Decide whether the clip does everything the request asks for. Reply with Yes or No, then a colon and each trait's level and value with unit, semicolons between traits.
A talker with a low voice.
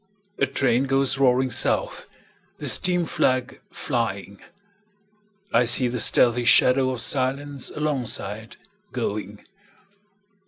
Yes: low, 130 Hz